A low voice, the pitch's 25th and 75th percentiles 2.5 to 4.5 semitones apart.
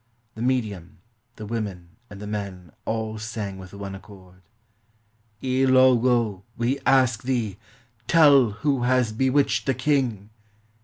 Yes: low, 110 Hz; average, 4.2 semitones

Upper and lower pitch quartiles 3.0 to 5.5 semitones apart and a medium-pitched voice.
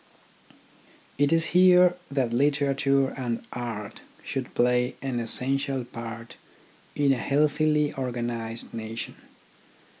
No: average, 3.3 semitones; low, 130 Hz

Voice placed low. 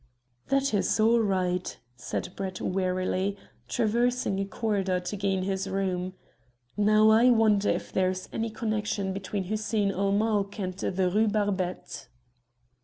No: high, 200 Hz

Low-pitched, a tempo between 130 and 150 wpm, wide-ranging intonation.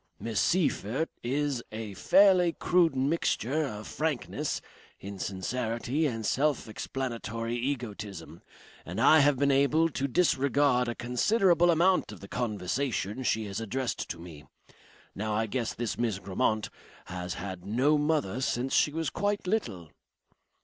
Yes: low, 125 Hz; slow, 135 wpm; wide, 5.8 semitones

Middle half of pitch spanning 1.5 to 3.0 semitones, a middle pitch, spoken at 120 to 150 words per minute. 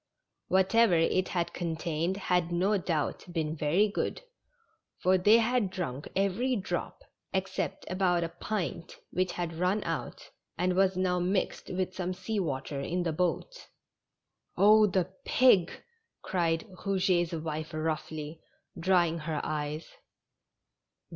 Yes: average, 2.7 semitones; medium, 180 Hz; slow, 135 wpm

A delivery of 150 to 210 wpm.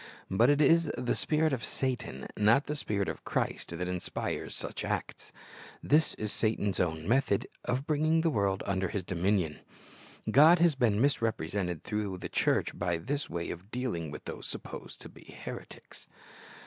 Yes: average, 165 wpm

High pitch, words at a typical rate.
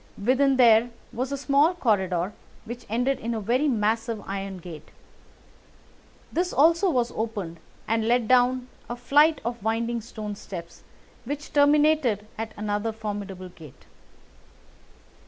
No: high, 230 Hz; slow, 130 wpm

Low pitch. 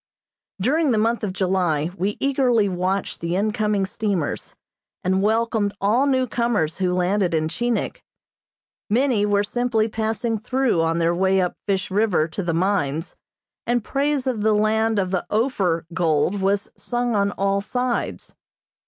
No: high, 205 Hz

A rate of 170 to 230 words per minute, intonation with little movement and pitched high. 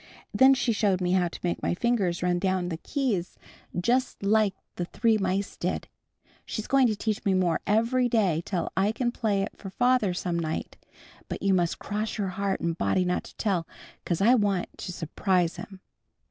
No: average, 195 wpm; average, 3.7 semitones; high, 195 Hz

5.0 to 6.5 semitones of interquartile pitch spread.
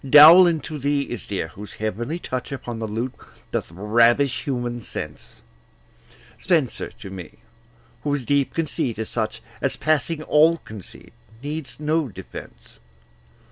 Yes: average, 5.3 semitones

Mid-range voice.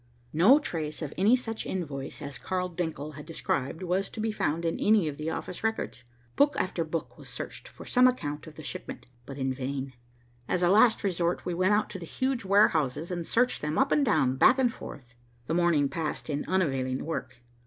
Yes: medium, 170 Hz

